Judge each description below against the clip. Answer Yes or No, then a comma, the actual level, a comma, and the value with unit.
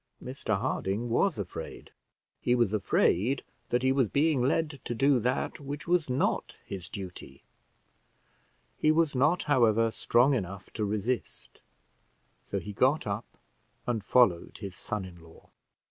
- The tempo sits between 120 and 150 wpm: Yes, average, 145 wpm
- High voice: No, low, 120 Hz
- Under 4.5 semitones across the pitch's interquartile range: No, average, 5.3 semitones